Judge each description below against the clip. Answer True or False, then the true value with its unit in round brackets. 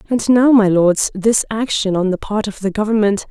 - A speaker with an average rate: False (220 wpm)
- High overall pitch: True (210 Hz)